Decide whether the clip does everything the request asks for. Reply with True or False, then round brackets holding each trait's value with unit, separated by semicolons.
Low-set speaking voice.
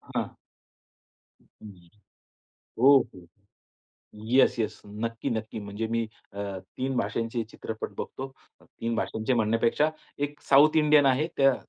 True (115 Hz)